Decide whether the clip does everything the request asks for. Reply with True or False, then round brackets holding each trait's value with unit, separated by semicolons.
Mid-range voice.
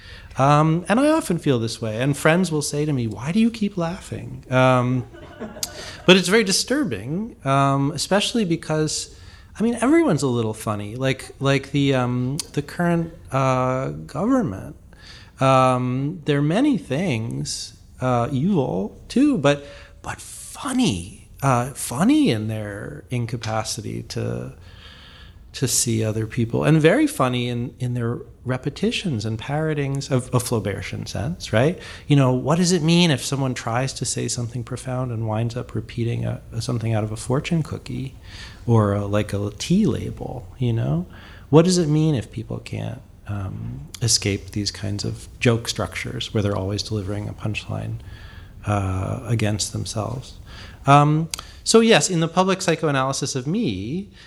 False (125 Hz)